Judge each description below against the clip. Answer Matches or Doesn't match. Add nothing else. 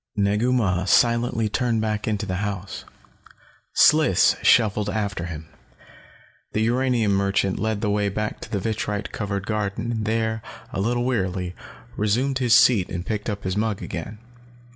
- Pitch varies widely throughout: Doesn't match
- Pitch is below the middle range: Matches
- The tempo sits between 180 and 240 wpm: Doesn't match